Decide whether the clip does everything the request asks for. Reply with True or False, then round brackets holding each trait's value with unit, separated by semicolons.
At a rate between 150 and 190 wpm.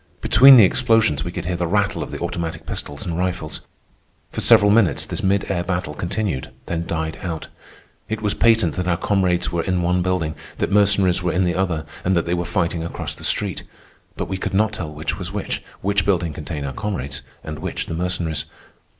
False (205 wpm)